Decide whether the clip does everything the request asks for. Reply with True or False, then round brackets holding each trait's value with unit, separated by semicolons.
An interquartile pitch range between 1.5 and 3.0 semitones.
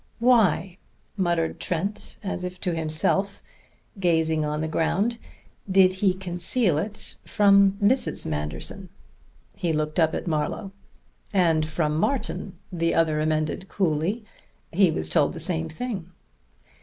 False (3.9 semitones)